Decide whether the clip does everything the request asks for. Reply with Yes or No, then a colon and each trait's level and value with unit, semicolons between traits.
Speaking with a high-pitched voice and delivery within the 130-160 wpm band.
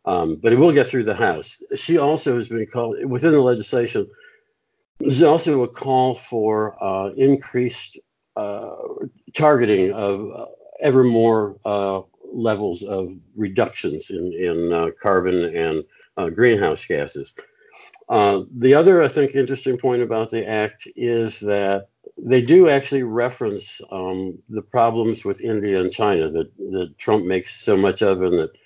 No: low, 115 Hz; average, 155 wpm